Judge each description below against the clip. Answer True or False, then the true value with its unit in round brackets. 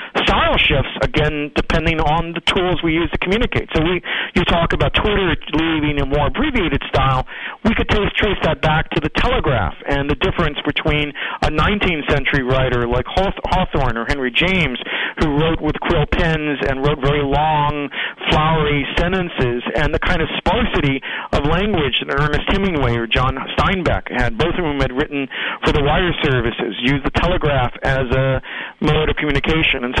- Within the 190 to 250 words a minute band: False (180 wpm)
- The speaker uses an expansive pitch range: False (3.5 semitones)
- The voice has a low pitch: False (150 Hz)